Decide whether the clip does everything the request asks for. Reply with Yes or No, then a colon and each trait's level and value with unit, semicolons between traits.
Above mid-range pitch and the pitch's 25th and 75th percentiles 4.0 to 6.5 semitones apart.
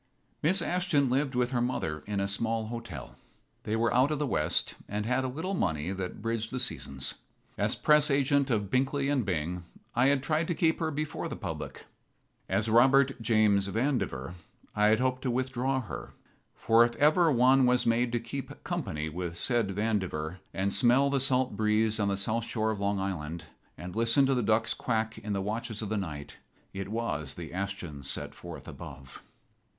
No: low, 115 Hz; average, 5.0 semitones